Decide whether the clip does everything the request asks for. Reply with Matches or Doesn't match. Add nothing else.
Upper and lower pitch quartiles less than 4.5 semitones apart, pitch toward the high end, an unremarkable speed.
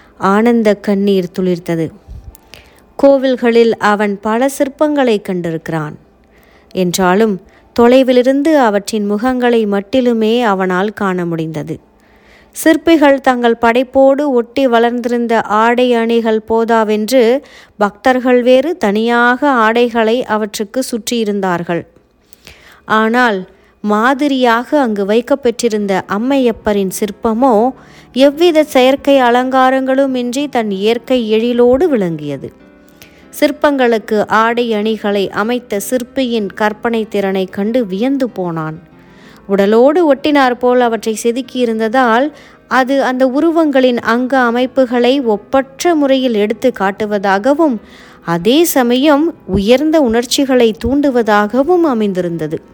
Matches